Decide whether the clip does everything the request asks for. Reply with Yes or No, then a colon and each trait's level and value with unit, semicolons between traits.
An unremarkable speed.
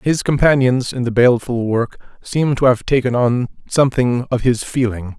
Yes: average, 175 wpm